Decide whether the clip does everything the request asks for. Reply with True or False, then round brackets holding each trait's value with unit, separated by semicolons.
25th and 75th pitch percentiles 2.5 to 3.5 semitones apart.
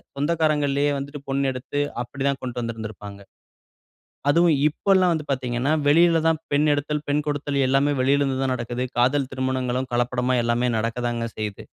True (3.0 semitones)